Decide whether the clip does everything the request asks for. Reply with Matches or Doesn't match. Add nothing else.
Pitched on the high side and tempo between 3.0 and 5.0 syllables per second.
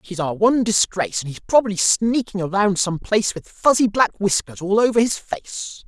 Doesn't match